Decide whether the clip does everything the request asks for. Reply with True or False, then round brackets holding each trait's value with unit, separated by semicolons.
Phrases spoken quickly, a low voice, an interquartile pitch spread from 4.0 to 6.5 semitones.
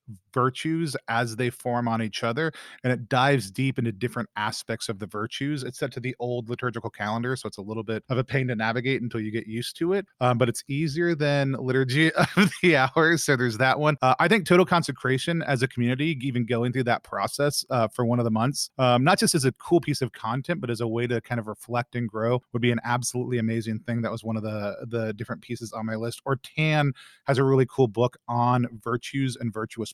False (240 wpm; 125 Hz; 3.2 semitones)